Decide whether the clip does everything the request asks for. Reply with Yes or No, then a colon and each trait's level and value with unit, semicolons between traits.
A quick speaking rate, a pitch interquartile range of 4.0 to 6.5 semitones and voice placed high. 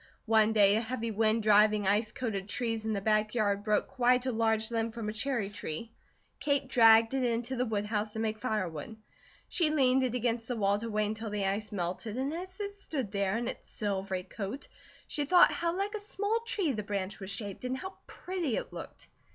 No: fast, 210 wpm; average, 3.6 semitones; high, 225 Hz